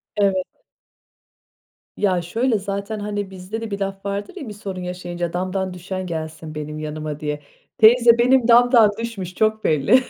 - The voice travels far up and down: No, average, 3.9 semitones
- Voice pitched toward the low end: No, high, 195 Hz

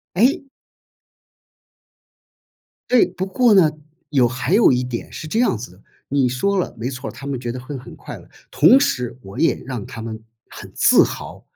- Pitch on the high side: No, low, 130 Hz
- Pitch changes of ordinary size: No, wide, 7.4 semitones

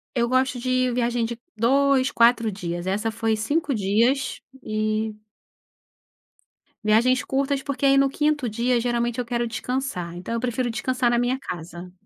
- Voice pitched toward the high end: Yes, high, 240 Hz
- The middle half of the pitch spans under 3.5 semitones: Yes, average, 2.9 semitones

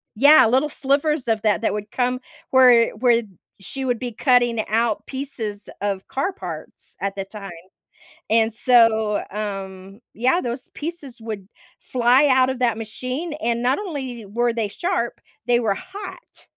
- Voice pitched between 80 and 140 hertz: No, high, 235 Hz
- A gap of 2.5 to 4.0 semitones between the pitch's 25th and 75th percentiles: Yes, average, 3.5 semitones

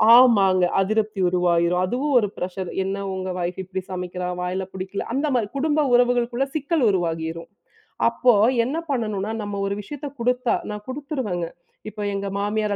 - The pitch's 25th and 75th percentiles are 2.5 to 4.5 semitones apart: No, average, 5.1 semitones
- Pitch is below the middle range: No, high, 205 Hz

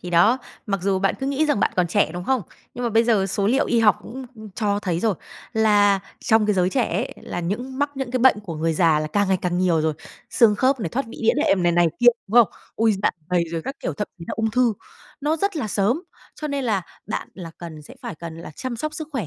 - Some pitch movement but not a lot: No, wide, 6.0 semitones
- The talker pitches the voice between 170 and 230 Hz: Yes, high, 210 Hz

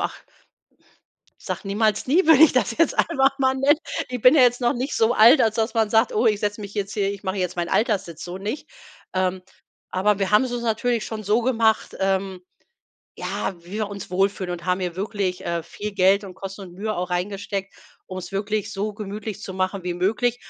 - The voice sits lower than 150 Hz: No, high, 205 Hz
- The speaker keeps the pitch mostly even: No, average, 3.3 semitones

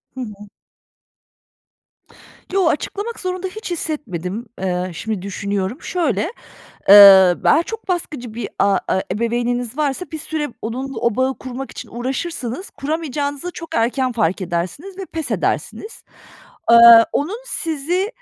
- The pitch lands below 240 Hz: No, very high, 260 Hz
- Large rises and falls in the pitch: Yes, wide, 7.6 semitones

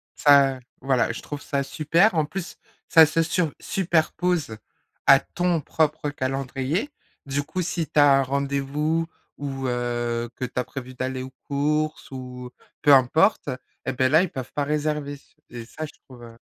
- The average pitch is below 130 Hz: No, medium, 140 Hz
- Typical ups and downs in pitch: Yes, average, 3.2 semitones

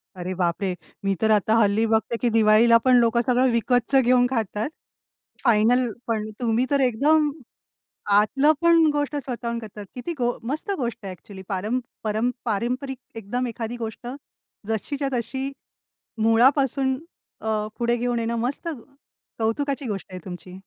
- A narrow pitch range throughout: No, average, 3.1 semitones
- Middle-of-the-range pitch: No, high, 235 Hz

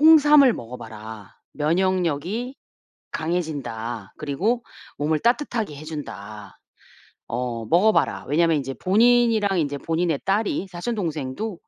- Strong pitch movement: Yes, wide, 7.9 semitones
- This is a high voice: No, medium, 165 Hz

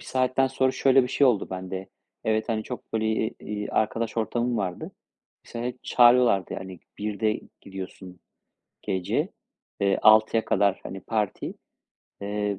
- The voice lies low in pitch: Yes, low, 110 Hz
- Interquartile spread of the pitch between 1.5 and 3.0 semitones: No, average, 3.6 semitones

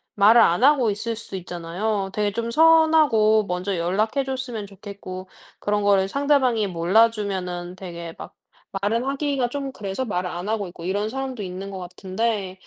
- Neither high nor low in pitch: No, high, 205 Hz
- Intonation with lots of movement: No, average, 4.1 semitones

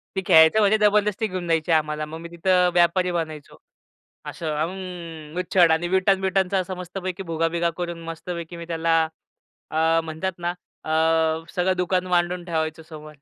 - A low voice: No, medium, 170 Hz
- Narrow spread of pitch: Yes, narrow, 2.3 semitones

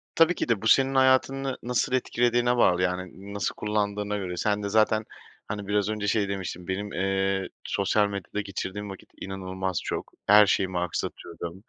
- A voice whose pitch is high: No, low, 100 Hz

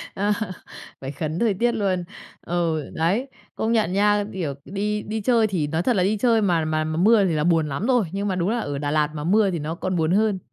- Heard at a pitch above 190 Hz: No, medium, 185 Hz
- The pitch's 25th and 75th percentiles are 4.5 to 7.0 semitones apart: Yes, average, 4.8 semitones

